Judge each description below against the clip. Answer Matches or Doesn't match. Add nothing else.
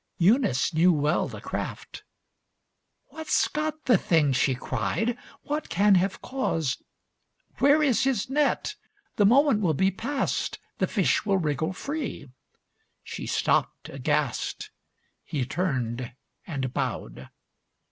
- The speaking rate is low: Matches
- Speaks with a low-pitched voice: Doesn't match